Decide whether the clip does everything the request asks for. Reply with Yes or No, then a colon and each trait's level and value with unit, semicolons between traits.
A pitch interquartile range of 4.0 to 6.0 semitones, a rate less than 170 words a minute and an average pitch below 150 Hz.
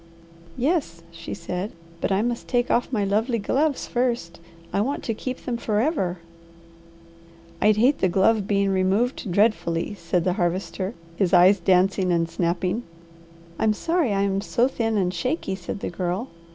No: average, 4.6 semitones; average, 160 wpm; high, 200 Hz